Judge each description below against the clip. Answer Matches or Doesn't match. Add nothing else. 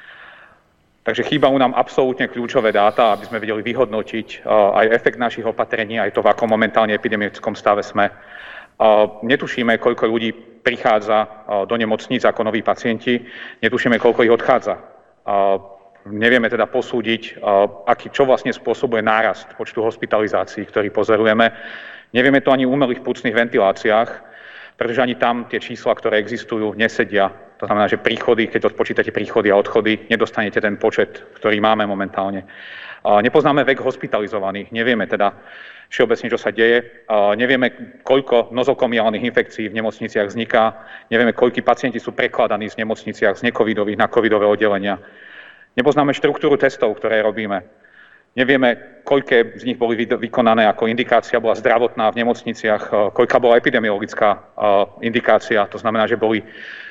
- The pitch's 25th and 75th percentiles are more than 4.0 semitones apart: Doesn't match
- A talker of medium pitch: Doesn't match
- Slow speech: Doesn't match